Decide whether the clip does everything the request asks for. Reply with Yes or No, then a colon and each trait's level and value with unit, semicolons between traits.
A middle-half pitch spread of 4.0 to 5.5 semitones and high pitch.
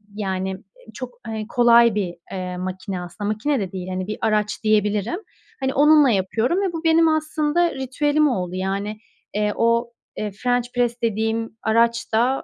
Yes: average, 4.6 semitones; high, 225 Hz